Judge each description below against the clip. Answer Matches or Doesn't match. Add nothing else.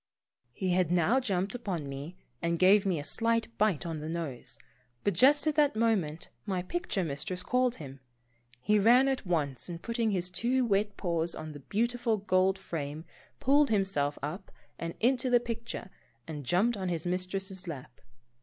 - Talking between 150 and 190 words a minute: Matches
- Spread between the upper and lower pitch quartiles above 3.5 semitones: Matches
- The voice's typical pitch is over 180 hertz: Matches